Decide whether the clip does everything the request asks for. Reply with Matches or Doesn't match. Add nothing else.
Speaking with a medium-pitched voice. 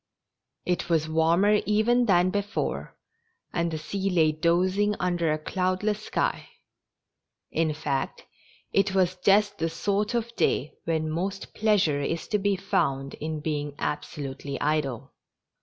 Matches